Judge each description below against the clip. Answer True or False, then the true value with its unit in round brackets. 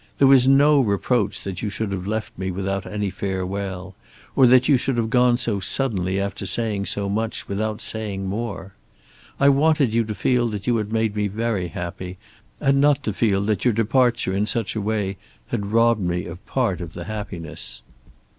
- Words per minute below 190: False (195 wpm)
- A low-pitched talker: True (105 Hz)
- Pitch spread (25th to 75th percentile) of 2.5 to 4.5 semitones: True (3.5 semitones)